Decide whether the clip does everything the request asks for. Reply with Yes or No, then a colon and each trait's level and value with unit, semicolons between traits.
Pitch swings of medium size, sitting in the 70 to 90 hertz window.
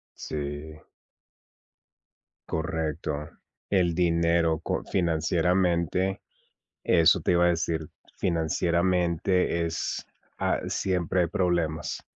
No: narrow, 1.8 semitones; very low, 85 Hz